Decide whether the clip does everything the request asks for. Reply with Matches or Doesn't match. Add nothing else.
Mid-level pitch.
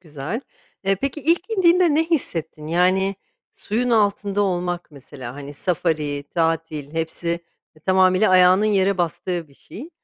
Matches